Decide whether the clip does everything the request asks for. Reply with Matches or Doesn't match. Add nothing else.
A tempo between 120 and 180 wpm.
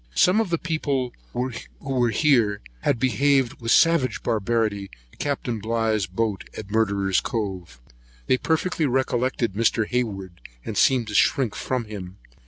Matches